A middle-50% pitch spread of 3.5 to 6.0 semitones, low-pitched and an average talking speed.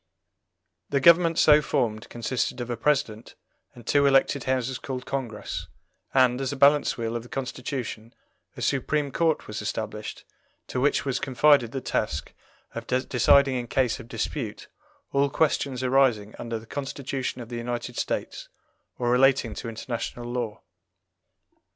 No: average, 2.8 semitones; low, 125 Hz; average, 150 wpm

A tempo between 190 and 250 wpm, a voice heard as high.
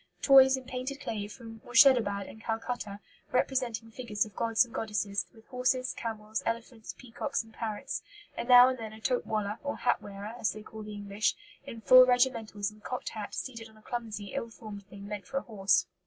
Yes: average, 200 wpm; high, 225 Hz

